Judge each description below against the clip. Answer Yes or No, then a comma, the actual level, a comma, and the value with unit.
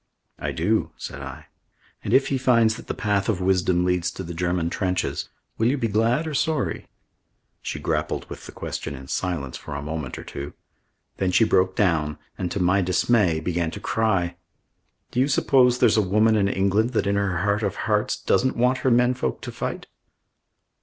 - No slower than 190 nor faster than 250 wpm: Yes, average, 195 wpm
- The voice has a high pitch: No, low, 100 Hz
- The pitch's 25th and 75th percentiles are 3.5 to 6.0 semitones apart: Yes, average, 4.5 semitones